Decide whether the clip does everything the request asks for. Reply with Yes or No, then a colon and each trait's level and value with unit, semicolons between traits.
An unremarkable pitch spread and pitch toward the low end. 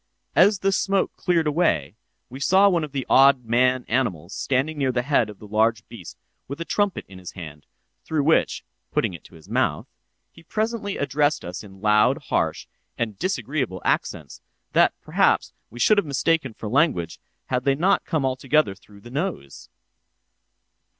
No: wide, 7.1 semitones; low, 130 Hz